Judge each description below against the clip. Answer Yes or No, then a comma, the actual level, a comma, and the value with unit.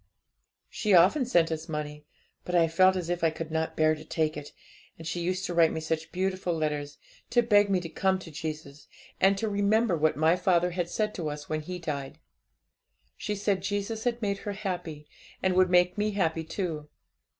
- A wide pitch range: No, average, 3.7 semitones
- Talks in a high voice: No, medium, 175 Hz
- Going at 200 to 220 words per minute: Yes, fast, 205 wpm